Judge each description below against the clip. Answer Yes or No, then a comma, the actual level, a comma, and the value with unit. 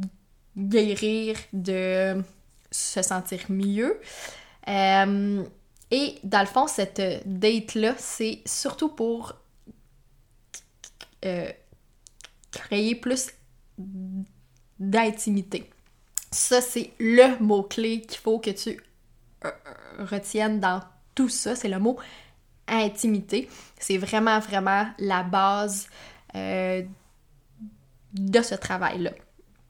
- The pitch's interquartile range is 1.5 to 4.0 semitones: Yes, average, 2.9 semitones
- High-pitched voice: Yes, high, 205 Hz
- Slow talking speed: Yes, slow, 90 wpm